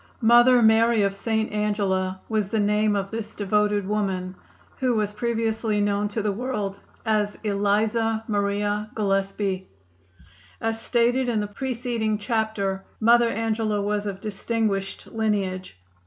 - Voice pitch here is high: Yes, high, 210 Hz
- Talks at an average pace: No, slow, 130 wpm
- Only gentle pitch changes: Yes, narrow, 1.9 semitones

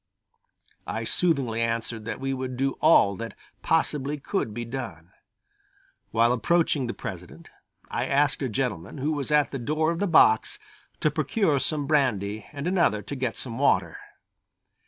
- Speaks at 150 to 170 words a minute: Yes, average, 155 wpm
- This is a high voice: No, low, 135 Hz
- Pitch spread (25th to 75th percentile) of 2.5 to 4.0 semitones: No, average, 4.6 semitones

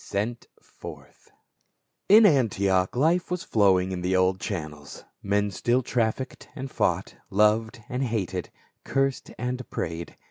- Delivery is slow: Yes, slow, 130 wpm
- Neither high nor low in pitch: No, low, 110 Hz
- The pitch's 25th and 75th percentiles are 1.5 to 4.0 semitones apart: No, average, 5.2 semitones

